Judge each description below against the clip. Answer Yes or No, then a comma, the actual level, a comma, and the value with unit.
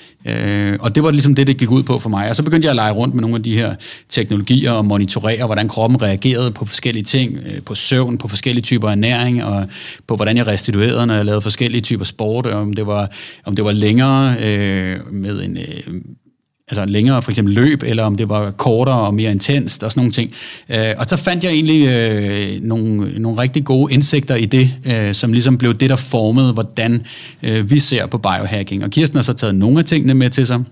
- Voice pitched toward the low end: Yes, low, 115 Hz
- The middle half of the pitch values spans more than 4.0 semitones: No, average, 3.6 semitones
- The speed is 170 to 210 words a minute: No, fast, 225 wpm